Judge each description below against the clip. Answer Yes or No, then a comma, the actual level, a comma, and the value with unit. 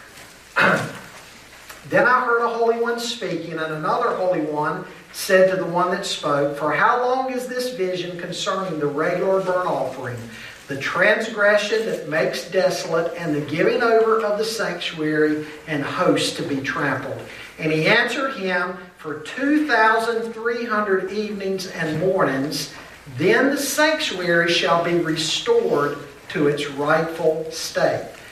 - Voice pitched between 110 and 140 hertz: No, medium, 180 Hz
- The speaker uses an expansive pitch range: Yes, wide, 6.2 semitones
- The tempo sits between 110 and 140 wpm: Yes, slow, 135 wpm